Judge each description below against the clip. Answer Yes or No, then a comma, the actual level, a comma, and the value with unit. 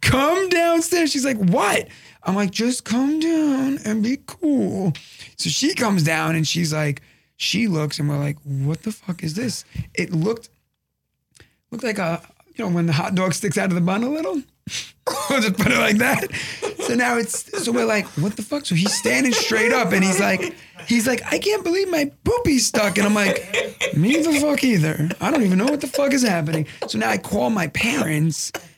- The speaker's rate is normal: No, fast, 210 wpm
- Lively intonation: Yes, wide, 8.3 semitones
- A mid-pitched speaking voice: No, high, 220 Hz